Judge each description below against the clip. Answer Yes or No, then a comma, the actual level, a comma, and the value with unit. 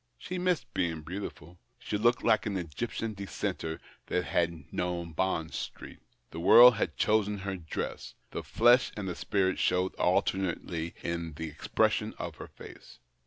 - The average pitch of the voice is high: No, very low, 90 Hz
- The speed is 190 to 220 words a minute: No, average, 155 wpm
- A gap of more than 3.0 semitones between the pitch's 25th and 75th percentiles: Yes, average, 4.1 semitones